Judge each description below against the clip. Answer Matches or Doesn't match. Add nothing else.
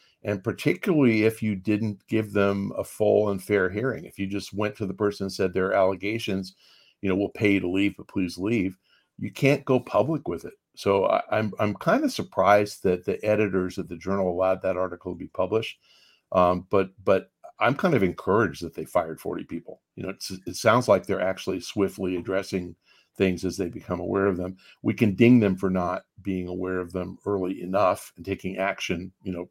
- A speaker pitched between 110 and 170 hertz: Doesn't match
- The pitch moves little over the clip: Matches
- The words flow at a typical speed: Doesn't match